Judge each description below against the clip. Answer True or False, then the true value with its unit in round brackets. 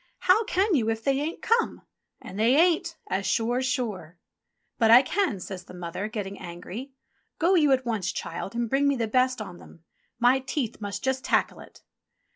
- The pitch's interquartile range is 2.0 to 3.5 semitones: False (5.6 semitones)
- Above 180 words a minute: True (190 wpm)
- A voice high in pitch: True (245 Hz)